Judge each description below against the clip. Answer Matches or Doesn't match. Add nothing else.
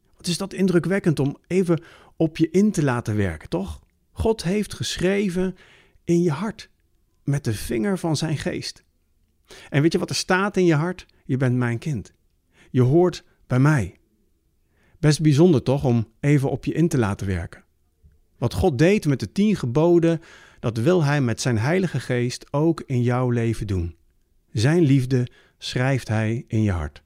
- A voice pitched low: Matches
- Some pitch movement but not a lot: Doesn't match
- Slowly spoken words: Doesn't match